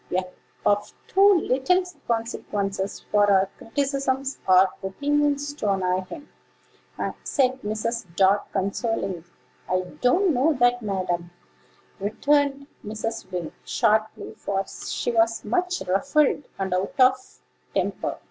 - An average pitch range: No, wide, 6.0 semitones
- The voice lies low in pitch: No, high, 225 Hz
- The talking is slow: Yes, slow, 120 wpm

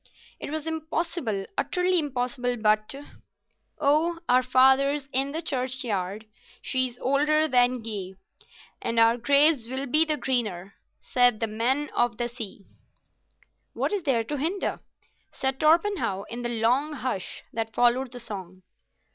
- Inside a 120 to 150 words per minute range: Yes, average, 140 wpm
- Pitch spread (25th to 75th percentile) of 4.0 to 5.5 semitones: Yes, average, 4.4 semitones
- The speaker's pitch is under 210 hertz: No, very high, 255 Hz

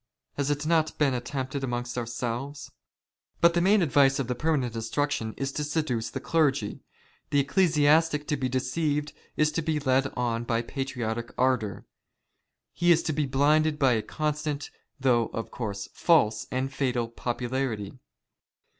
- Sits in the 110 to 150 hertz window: Yes, low, 135 Hz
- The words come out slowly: No, average, 155 wpm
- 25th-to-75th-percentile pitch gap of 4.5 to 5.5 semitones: No, average, 3.7 semitones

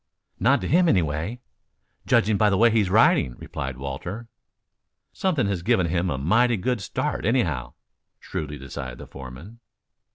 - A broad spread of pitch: Yes, wide, 8.5 semitones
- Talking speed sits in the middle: Yes, average, 155 wpm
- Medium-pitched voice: No, very low, 90 Hz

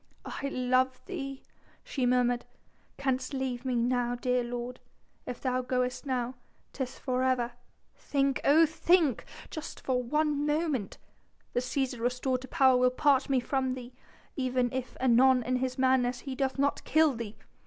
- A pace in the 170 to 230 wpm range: No, average, 155 wpm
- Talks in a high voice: Yes, very high, 255 Hz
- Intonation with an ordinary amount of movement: No, narrow, 1.6 semitones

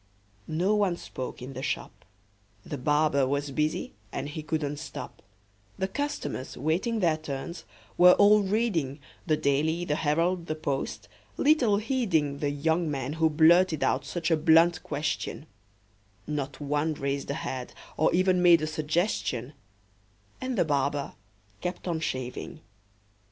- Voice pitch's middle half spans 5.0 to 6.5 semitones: No, average, 3.7 semitones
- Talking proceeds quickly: No, average, 145 wpm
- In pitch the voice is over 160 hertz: No, medium, 155 Hz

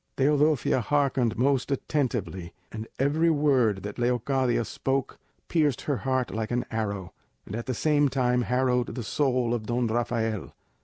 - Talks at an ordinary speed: Yes, average, 150 wpm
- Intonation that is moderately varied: Yes, average, 3.4 semitones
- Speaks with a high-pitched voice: No, low, 125 Hz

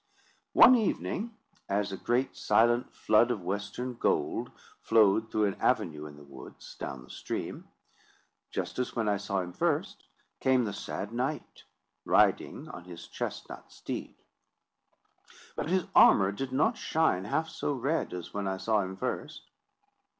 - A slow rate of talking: No, average, 150 wpm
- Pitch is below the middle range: Yes, low, 105 Hz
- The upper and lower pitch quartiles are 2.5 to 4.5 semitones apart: No, average, 5.2 semitones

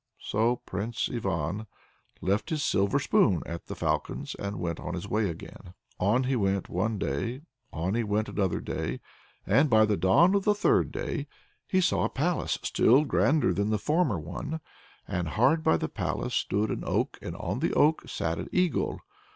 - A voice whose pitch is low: Yes, low, 110 Hz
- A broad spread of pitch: Yes, wide, 7.0 semitones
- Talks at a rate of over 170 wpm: Yes, average, 185 wpm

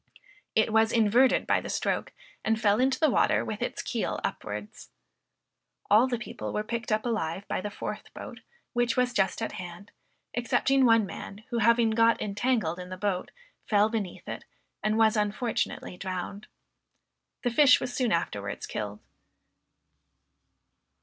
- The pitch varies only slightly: No, average, 3.0 semitones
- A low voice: No, high, 220 Hz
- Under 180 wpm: Yes, average, 155 wpm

